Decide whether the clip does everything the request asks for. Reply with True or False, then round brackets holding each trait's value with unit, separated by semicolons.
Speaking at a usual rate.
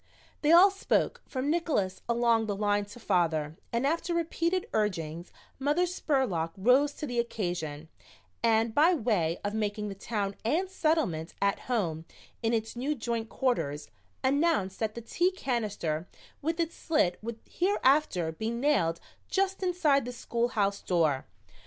True (145 wpm)